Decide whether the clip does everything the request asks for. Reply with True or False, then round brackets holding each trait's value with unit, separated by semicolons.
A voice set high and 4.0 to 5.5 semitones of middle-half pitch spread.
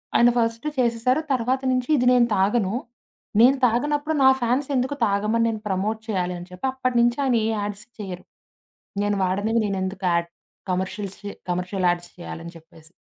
True (215 Hz; 4.5 semitones)